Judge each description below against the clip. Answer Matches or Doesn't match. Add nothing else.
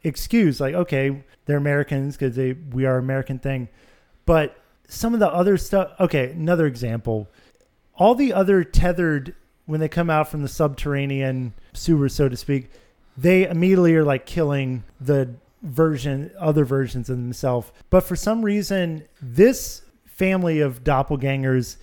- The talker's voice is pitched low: Doesn't match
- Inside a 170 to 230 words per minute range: Doesn't match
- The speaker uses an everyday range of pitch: Matches